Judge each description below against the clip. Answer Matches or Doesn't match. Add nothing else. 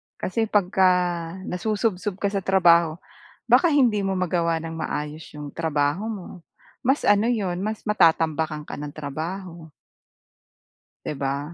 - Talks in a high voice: Doesn't match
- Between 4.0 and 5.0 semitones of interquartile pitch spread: Matches